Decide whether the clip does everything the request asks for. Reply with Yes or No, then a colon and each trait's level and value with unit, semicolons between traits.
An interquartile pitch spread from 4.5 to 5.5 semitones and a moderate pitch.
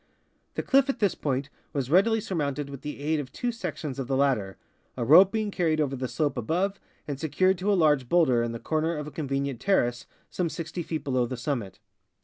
Yes: average, 5.0 semitones; medium, 150 Hz